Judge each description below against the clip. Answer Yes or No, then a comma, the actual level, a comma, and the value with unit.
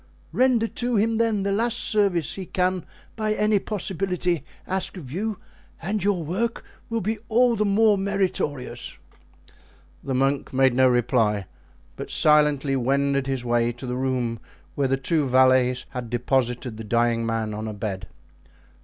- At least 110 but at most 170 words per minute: Yes, average, 155 wpm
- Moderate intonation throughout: No, wide, 8.3 semitones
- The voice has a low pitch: No, medium, 145 Hz